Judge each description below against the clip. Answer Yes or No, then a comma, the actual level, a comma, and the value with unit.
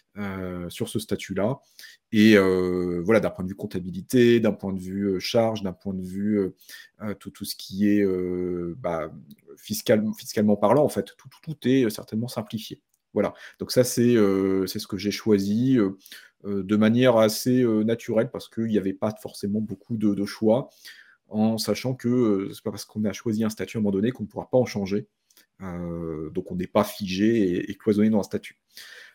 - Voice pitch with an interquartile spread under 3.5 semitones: Yes, average, 2.8 semitones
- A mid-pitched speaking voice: No, low, 105 Hz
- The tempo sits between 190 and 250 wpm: Yes, average, 210 wpm